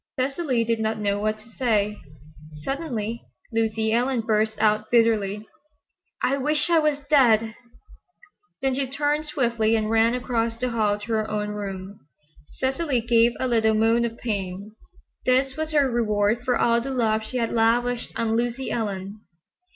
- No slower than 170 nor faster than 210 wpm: No, average, 160 wpm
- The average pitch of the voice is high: Yes, high, 230 Hz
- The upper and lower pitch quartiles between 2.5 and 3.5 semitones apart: Yes, average, 2.9 semitones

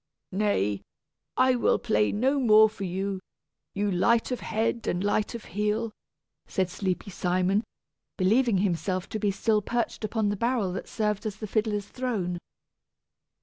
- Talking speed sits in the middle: Yes, average, 150 wpm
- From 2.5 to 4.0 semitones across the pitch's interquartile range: Yes, average, 3.0 semitones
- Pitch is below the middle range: No, high, 210 Hz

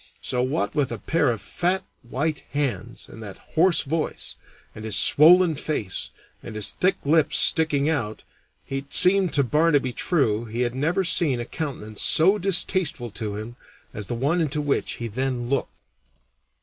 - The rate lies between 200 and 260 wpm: No, average, 165 wpm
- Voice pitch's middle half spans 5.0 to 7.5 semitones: Yes, wide, 5.4 semitones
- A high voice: No, medium, 140 Hz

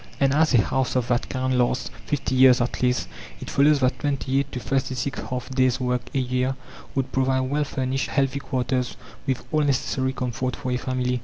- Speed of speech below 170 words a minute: No, average, 190 wpm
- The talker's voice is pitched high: No, low, 130 Hz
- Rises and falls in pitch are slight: Yes, narrow, 1.2 semitones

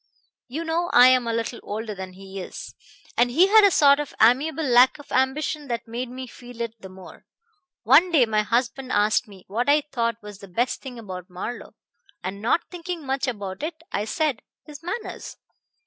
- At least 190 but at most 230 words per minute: Yes, average, 195 wpm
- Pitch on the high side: Yes, high, 245 Hz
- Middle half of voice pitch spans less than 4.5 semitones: No, wide, 5.6 semitones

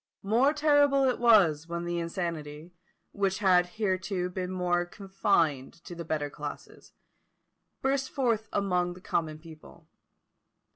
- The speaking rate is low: Yes, slow, 130 wpm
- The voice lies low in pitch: No, medium, 180 Hz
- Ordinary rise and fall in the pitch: Yes, average, 4.1 semitones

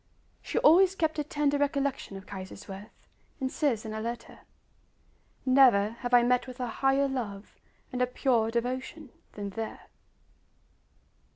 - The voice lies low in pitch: No, very high, 250 Hz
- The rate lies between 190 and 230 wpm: No, average, 145 wpm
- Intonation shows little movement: No, average, 4.1 semitones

